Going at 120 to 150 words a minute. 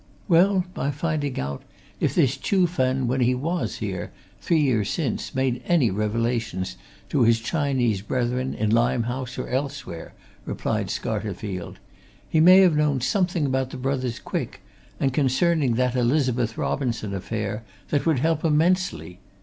Yes: average, 145 wpm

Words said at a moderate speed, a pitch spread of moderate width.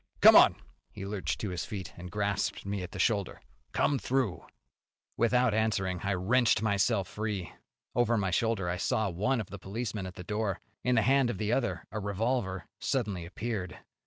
Yes: average, 185 wpm; average, 3.6 semitones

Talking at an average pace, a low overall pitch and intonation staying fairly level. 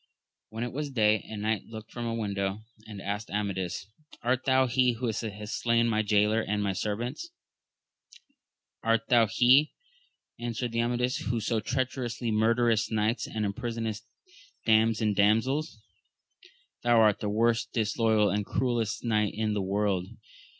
Yes: average, 145 wpm; low, 110 Hz; narrow, 2.2 semitones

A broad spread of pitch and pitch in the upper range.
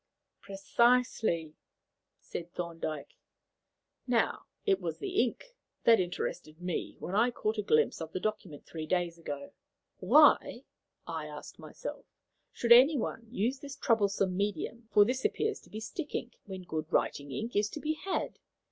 Yes: wide, 6.0 semitones; high, 205 Hz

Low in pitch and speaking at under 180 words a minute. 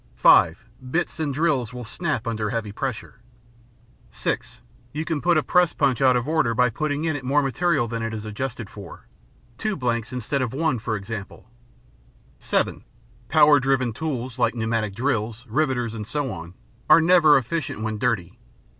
Yes: low, 125 Hz; average, 165 wpm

